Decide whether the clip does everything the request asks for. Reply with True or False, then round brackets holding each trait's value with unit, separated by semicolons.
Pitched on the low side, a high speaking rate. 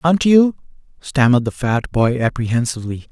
False (130 Hz; 135 wpm)